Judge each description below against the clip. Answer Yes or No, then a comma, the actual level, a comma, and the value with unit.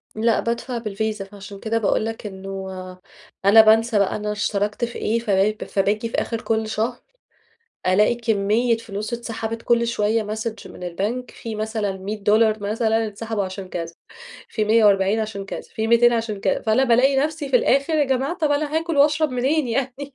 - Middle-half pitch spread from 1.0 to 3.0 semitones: Yes, narrow, 2.5 semitones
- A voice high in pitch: Yes, high, 220 Hz